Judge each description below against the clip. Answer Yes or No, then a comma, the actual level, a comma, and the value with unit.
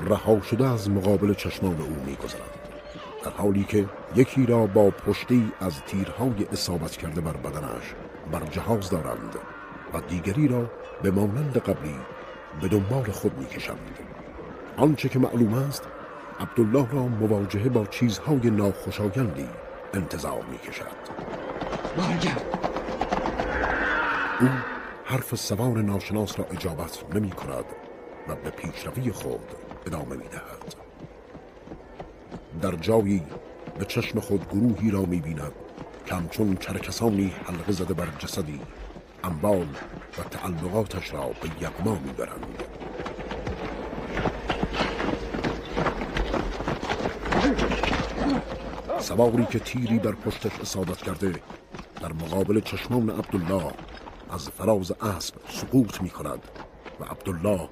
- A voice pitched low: Yes, low, 100 Hz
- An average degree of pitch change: Yes, average, 3.9 semitones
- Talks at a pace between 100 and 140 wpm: Yes, average, 110 wpm